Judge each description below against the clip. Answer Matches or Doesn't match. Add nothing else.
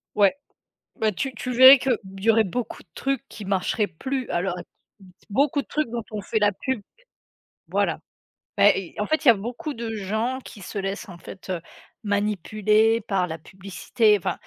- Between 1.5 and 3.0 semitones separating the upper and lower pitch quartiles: Doesn't match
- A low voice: Doesn't match